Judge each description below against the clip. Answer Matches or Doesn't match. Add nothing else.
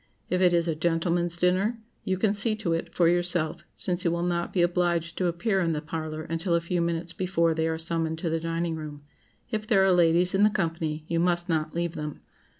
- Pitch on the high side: Doesn't match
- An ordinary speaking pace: Doesn't match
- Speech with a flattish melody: Matches